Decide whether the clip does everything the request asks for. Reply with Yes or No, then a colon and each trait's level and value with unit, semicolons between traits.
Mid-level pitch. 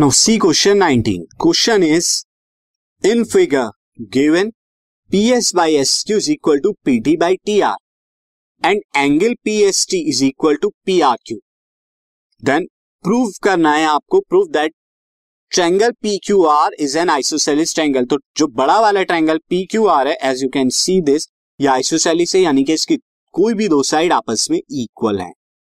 No: high, 200 Hz